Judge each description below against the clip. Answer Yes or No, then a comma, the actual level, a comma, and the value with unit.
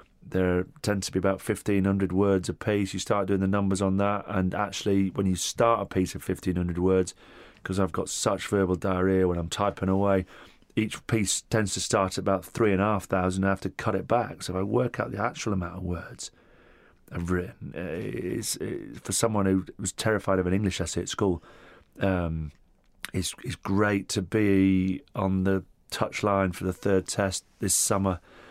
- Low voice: Yes, very low, 95 Hz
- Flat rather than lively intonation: Yes, narrow, 1.4 semitones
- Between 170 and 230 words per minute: Yes, average, 200 wpm